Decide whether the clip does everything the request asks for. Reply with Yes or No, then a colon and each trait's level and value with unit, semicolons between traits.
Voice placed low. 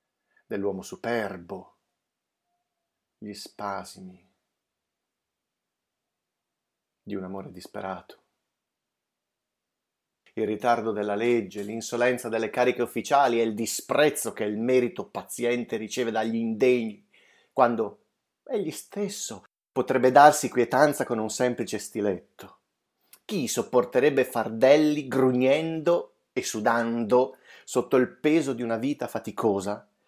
Yes: low, 120 Hz